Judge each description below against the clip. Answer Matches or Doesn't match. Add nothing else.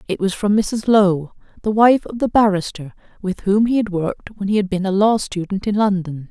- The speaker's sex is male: Doesn't match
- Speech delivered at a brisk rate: Matches